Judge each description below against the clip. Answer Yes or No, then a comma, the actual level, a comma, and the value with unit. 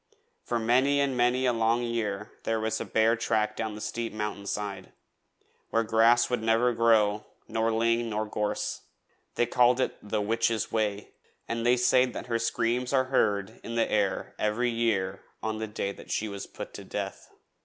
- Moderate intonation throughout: No, narrow, 1.9 semitones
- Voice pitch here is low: Yes, low, 115 Hz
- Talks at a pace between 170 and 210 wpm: Yes, average, 180 wpm